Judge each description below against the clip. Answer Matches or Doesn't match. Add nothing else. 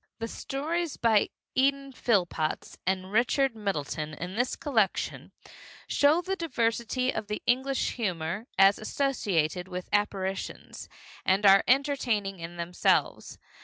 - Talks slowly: Matches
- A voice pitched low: Doesn't match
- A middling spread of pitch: Doesn't match